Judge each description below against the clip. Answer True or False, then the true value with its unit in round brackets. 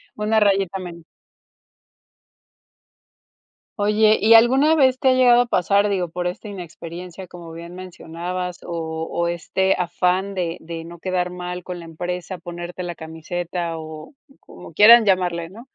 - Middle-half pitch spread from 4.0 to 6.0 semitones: False (2.9 semitones)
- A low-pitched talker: False (180 Hz)